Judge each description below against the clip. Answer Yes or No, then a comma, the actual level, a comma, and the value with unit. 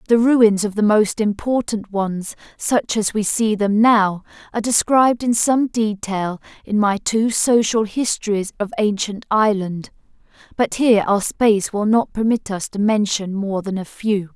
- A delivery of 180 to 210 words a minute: No, average, 160 wpm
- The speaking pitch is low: No, high, 210 Hz